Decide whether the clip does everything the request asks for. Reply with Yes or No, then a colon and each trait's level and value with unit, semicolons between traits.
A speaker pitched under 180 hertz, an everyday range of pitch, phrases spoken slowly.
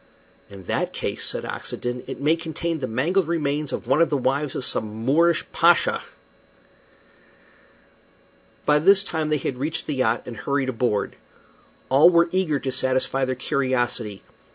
No: medium, 140 Hz; average, 4.2 semitones; average, 155 wpm